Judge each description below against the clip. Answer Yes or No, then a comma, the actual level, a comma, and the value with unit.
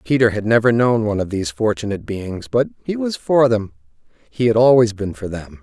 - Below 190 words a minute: No, fast, 205 wpm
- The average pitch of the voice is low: Yes, low, 110 Hz